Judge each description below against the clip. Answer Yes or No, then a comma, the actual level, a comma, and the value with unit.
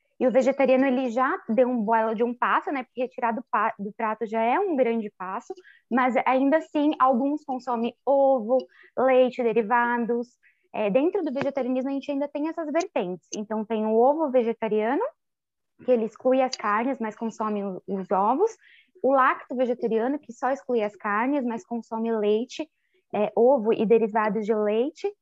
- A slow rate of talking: No, average, 165 wpm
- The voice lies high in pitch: Yes, very high, 250 Hz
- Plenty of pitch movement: No, average, 3.4 semitones